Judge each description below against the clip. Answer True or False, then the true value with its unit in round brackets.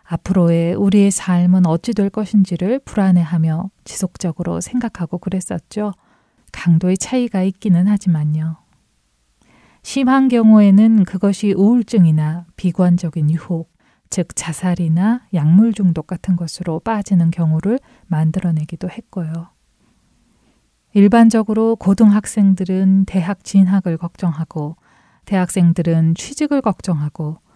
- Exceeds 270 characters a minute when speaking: True (280 characters per minute)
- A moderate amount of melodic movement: True (3.5 semitones)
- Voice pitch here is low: False (185 Hz)